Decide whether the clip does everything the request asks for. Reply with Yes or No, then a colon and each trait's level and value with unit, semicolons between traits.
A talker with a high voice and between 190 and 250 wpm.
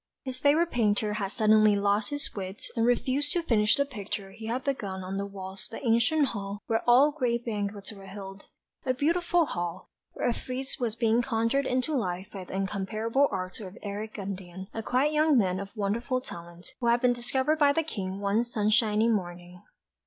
Yes: high, 220 Hz; average, 195 wpm